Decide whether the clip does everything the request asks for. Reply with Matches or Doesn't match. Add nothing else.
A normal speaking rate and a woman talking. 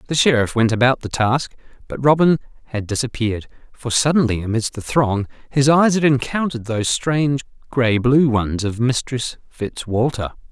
Doesn't match